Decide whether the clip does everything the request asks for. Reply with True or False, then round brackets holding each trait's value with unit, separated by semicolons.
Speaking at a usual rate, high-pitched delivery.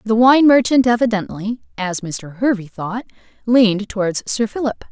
True (145 wpm; 220 Hz)